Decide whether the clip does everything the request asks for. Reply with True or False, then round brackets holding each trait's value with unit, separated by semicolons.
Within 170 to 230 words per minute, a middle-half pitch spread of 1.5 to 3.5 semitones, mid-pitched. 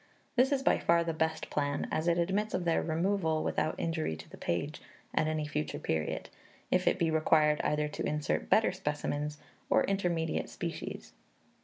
True (175 wpm; 2.4 semitones; 160 Hz)